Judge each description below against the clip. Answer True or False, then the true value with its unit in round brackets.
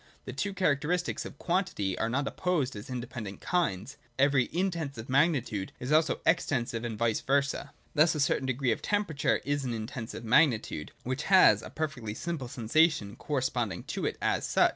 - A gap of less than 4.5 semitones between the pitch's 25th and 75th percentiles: False (5.3 semitones)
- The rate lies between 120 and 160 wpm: False (170 wpm)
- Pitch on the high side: False (135 Hz)